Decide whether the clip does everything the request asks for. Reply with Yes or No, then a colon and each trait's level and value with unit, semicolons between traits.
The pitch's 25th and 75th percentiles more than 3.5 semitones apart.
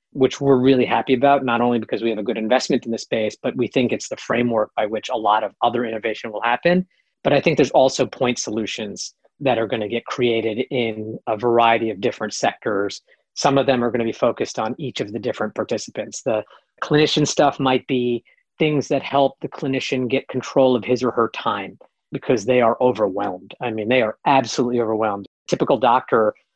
No: average, 2.7 semitones